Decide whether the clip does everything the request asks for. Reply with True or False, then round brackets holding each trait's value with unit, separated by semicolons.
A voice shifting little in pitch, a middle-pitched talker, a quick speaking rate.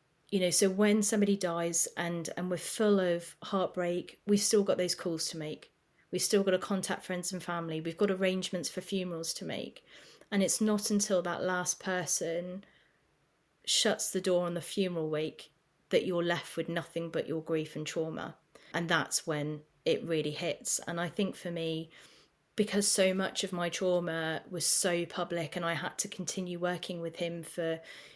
False (2.3 semitones; 175 Hz; 185 wpm)